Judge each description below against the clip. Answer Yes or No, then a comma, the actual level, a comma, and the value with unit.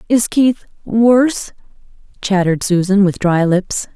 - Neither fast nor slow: No, slow, 105 wpm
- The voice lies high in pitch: Yes, high, 205 Hz